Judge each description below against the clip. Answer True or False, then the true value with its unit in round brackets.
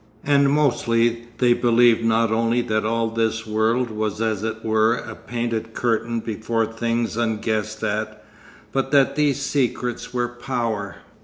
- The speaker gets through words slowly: False (145 wpm)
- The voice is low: True (115 Hz)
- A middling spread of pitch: False (1.6 semitones)